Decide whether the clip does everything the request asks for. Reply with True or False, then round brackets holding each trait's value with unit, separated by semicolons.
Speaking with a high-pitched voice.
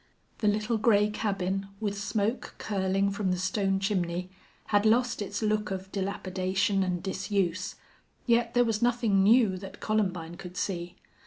True (200 Hz)